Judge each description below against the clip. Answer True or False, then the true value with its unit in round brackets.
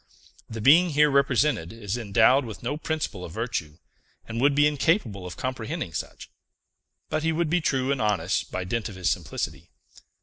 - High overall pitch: False (120 Hz)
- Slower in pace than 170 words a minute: False (175 wpm)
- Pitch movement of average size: False (6.2 semitones)